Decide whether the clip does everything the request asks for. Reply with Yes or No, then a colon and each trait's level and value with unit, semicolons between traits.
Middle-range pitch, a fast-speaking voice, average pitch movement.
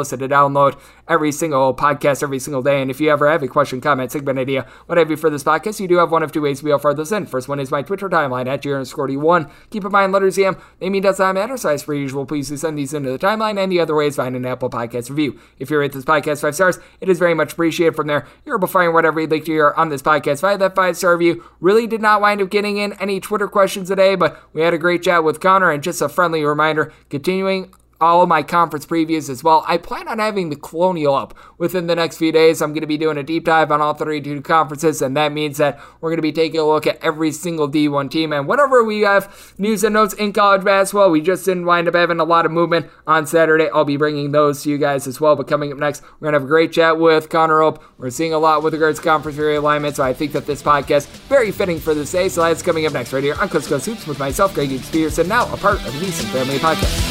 Yes: medium, 155 Hz; fast, 280 wpm; average, 3.2 semitones